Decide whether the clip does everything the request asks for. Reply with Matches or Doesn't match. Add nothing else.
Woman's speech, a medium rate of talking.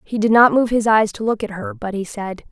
Doesn't match